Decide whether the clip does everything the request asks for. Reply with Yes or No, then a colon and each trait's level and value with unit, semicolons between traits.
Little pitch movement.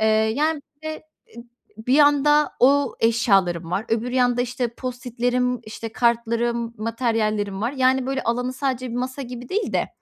Yes: narrow, 2.3 semitones